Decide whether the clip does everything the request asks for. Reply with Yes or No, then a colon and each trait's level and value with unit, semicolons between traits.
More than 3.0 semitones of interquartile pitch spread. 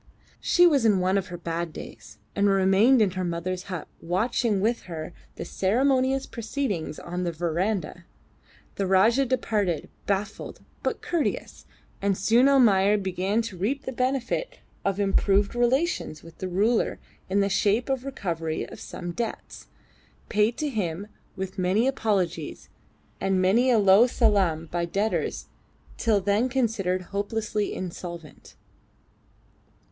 Yes: average, 4.4 semitones